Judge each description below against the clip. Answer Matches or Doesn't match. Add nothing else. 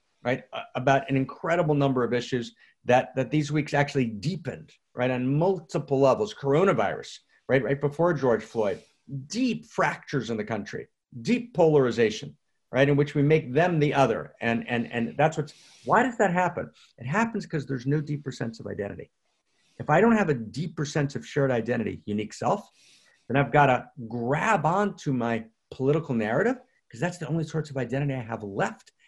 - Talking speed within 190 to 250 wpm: Doesn't match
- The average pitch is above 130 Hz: Matches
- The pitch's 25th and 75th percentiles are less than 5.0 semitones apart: Matches